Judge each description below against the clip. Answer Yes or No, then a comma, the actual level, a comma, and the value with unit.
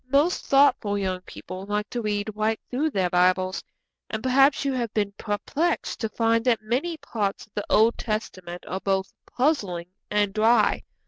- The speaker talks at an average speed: Yes, average, 170 wpm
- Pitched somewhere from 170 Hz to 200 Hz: No, high, 215 Hz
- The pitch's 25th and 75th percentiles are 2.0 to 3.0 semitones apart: No, average, 4.1 semitones